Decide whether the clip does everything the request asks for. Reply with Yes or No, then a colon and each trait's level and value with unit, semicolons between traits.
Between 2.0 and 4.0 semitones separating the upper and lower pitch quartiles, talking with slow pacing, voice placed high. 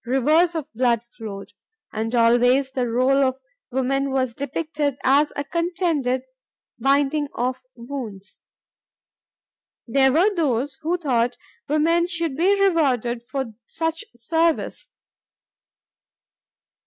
No: average, 4.5 semitones; slow, 105 wpm; very high, 270 Hz